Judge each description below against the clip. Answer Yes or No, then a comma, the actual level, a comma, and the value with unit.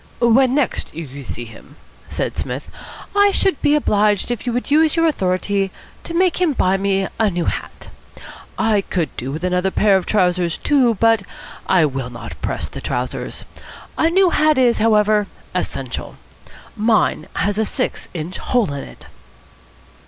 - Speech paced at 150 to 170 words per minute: Yes, average, 165 wpm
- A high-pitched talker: Yes, high, 210 Hz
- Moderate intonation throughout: No, wide, 6.3 semitones